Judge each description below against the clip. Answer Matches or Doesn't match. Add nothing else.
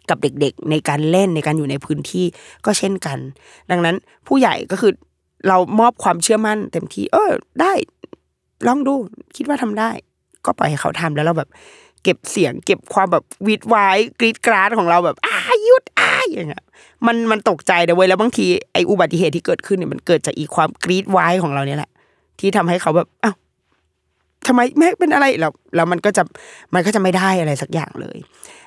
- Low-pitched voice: Doesn't match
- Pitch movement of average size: Doesn't match